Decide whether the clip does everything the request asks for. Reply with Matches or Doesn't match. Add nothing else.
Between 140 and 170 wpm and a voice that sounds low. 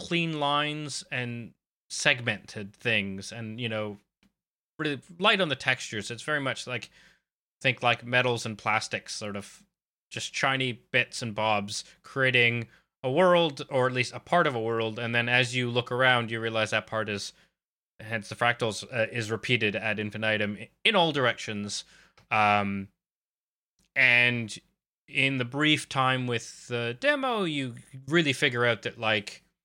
Matches